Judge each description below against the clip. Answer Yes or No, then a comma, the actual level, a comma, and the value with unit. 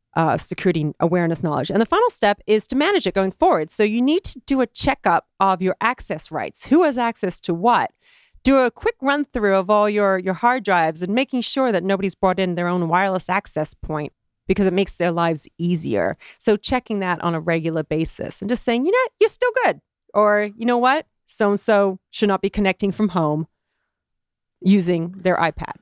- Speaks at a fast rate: Yes, fast, 210 wpm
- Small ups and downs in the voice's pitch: No, wide, 5.5 semitones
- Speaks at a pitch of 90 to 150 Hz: No, high, 200 Hz